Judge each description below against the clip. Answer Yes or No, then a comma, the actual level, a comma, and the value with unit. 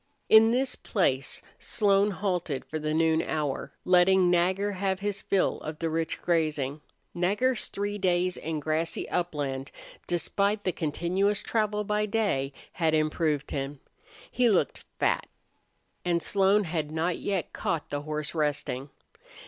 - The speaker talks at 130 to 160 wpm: Yes, average, 140 wpm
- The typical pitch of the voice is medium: Yes, medium, 175 Hz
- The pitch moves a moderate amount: Yes, average, 4.5 semitones